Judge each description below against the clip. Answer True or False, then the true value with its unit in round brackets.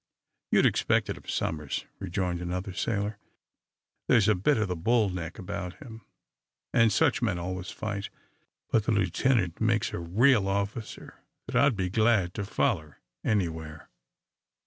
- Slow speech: False (145 wpm)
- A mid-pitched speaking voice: False (100 Hz)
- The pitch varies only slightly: False (3.9 semitones)